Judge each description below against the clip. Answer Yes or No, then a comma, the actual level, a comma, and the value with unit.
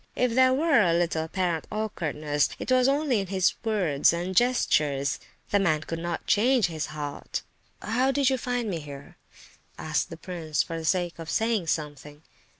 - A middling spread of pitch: No, wide, 6.8 semitones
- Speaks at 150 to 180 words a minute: Yes, average, 170 wpm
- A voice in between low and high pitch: Yes, medium, 175 Hz